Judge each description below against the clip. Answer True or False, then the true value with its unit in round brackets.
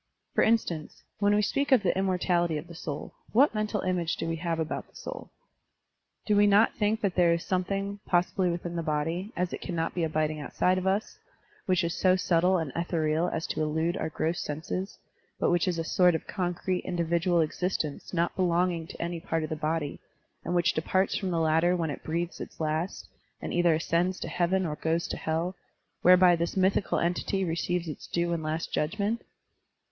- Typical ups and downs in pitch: False (2.3 semitones)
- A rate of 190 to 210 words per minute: True (205 wpm)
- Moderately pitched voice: True (175 Hz)